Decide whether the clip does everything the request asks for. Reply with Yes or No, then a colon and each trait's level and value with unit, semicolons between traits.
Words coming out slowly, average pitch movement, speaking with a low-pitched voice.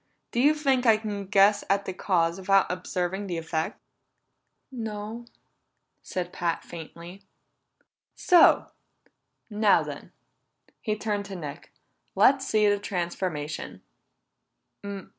No: slow, 110 wpm; average, 3.5 semitones; high, 200 Hz